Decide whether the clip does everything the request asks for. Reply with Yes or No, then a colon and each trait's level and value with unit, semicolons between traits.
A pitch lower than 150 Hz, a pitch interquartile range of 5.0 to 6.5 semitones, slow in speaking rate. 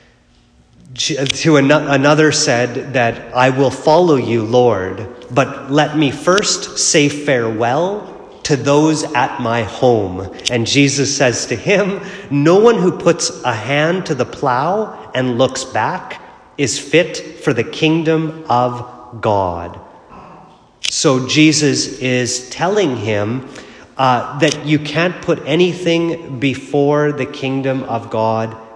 No: medium, 140 Hz; average, 4.2 semitones; slow, 125 wpm